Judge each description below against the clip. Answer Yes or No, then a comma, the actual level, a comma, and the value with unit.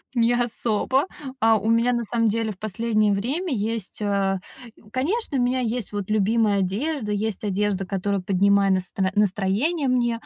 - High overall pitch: Yes, high, 215 Hz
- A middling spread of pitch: Yes, average, 3.3 semitones